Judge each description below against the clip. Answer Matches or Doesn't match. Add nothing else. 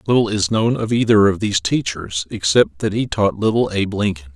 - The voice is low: Matches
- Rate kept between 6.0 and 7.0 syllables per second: Doesn't match